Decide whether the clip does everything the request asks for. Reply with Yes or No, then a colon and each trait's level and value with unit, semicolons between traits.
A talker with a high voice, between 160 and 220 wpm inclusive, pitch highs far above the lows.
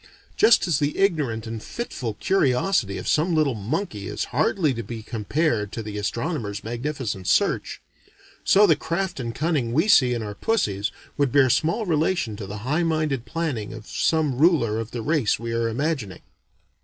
No: low, 130 Hz; average, 175 wpm; wide, 6.3 semitones